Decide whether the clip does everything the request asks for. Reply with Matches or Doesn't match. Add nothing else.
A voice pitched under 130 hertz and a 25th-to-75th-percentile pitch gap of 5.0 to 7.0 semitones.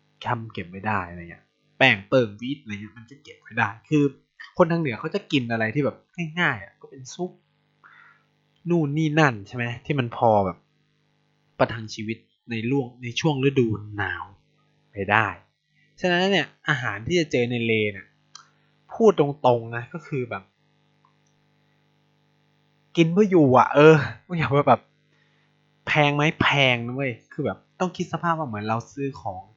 Doesn't match